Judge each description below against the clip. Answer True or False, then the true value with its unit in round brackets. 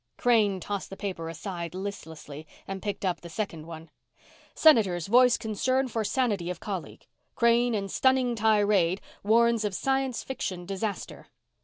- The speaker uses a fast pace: False (145 wpm)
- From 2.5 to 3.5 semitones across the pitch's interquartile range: False (4.7 semitones)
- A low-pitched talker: False (205 Hz)